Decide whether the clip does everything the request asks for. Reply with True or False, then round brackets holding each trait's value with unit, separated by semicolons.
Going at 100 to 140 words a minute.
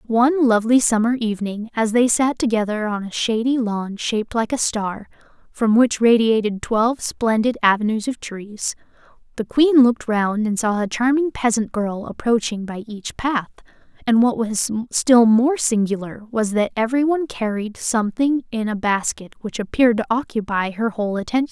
False (165 wpm)